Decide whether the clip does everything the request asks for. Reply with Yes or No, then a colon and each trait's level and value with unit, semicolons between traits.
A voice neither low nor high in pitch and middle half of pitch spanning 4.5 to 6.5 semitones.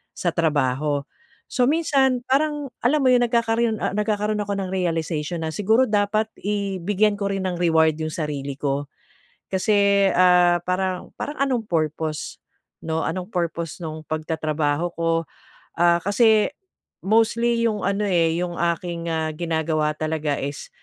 Yes: medium, 180 Hz; average, 4.9 semitones